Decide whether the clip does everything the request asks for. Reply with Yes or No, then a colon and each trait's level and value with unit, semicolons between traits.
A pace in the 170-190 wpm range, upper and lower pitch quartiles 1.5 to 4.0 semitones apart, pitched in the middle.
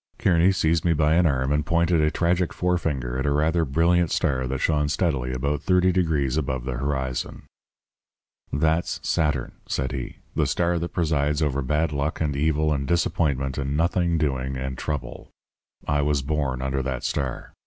No: average, 175 wpm; average, 3.6 semitones; very low, 75 Hz